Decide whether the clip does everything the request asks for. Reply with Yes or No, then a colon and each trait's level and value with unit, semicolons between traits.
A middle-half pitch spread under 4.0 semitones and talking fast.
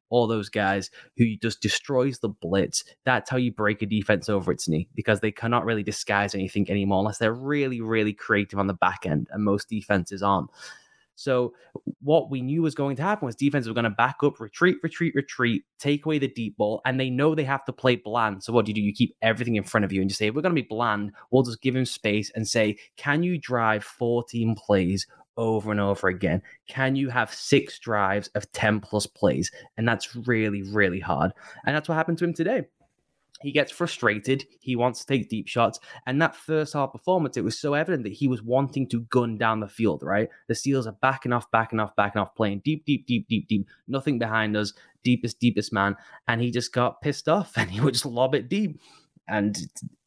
No: average, 4.3 semitones; fast, 225 wpm